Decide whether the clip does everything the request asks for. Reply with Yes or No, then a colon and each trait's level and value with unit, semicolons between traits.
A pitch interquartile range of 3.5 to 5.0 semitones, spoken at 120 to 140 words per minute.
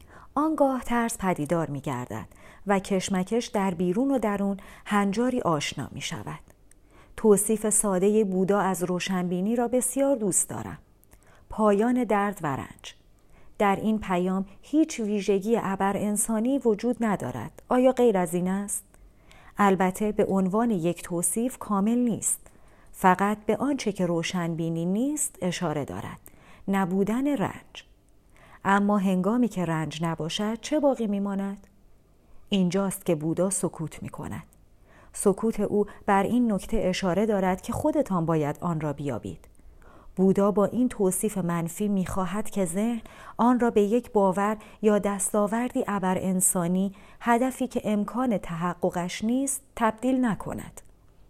Yes: average, 4.1 semitones; average, 130 wpm